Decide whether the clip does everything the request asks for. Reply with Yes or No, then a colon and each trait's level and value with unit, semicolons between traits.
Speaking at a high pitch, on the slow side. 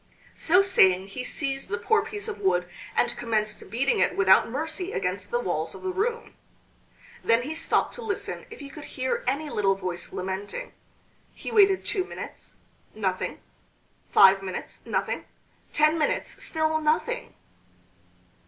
No: very high, 295 Hz; average, 150 wpm